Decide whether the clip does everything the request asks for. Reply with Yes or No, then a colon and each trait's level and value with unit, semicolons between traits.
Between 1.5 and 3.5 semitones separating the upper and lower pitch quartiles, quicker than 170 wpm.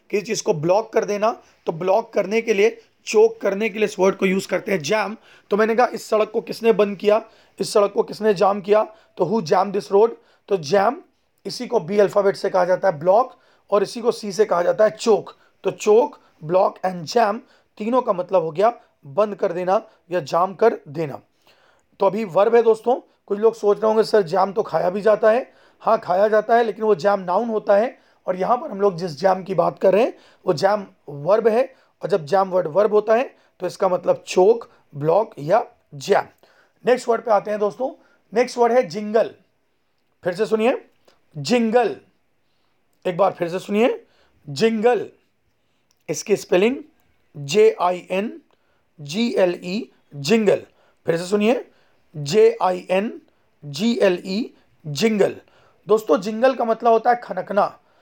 Yes: average, 3.2 semitones; fast, 190 wpm